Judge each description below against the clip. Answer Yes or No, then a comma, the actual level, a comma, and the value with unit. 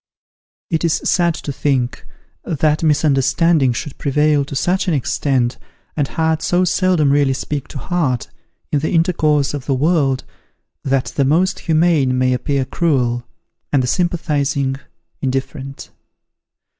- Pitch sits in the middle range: Yes, medium, 145 Hz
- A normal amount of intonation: Yes, average, 3.4 semitones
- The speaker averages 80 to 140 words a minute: Yes, slow, 135 wpm